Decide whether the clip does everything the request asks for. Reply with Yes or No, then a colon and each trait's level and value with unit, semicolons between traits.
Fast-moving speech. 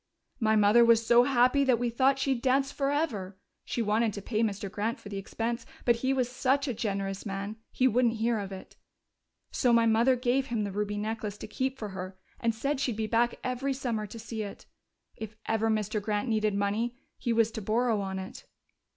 Yes: fast, 210 wpm